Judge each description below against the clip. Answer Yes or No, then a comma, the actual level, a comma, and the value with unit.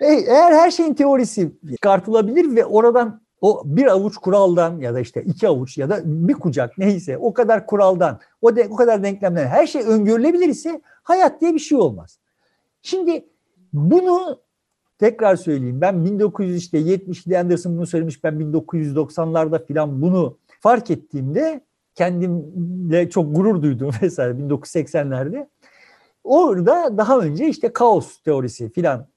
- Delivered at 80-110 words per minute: No, average, 135 wpm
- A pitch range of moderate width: No, wide, 6.8 semitones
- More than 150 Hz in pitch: Yes, medium, 185 Hz